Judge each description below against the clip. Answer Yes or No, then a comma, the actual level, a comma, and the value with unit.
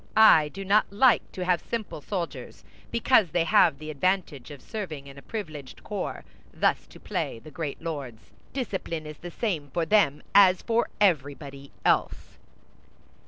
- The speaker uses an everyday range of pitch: No, wide, 5.7 semitones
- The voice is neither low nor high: Yes, medium, 165 Hz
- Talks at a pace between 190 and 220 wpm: No, average, 160 wpm